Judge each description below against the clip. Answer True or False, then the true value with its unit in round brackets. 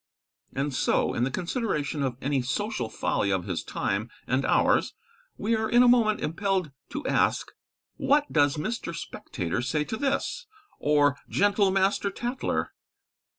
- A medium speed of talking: True (150 wpm)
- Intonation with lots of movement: True (8.3 semitones)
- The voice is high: False (170 Hz)